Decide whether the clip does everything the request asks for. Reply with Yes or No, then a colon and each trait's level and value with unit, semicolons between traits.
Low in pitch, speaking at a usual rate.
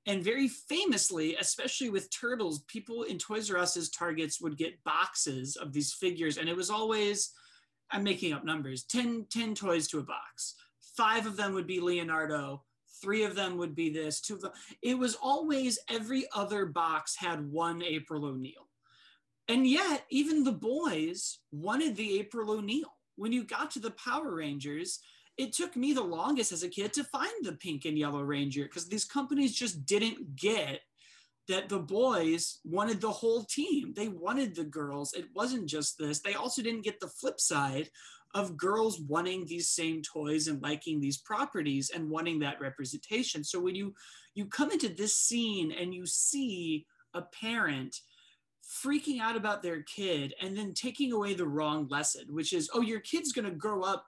No: high, 195 Hz; average, 180 wpm